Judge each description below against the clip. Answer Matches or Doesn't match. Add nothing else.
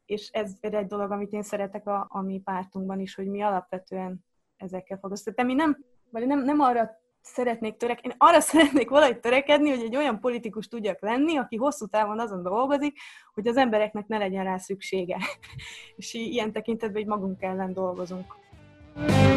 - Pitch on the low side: Doesn't match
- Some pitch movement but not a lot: Matches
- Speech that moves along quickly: Matches